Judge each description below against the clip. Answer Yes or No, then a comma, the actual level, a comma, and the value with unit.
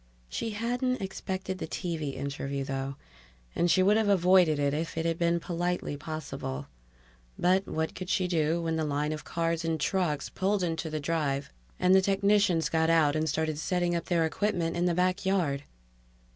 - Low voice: No, medium, 165 Hz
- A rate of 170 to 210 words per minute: Yes, average, 180 wpm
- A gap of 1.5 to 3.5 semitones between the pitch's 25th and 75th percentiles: Yes, average, 3.2 semitones